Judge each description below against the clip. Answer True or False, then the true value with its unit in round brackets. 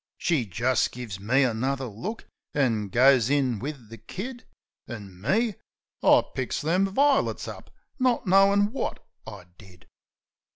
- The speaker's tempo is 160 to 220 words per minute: False (135 wpm)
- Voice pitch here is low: True (130 Hz)